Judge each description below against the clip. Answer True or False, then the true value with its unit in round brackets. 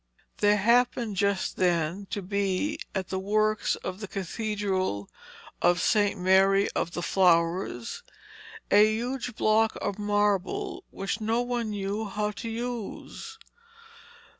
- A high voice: True (205 Hz)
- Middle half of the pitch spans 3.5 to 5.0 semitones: False (2.5 semitones)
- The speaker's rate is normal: False (125 wpm)